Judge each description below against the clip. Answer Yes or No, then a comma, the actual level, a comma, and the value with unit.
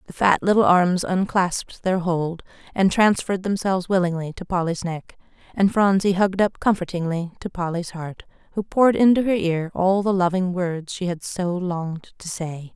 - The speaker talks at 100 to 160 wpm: No, average, 175 wpm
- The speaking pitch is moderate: Yes, medium, 180 Hz